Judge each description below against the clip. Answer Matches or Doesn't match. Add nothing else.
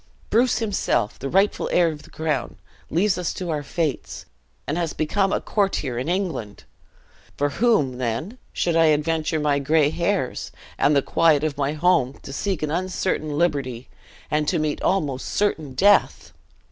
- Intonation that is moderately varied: Matches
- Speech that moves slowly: Doesn't match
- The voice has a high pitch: Doesn't match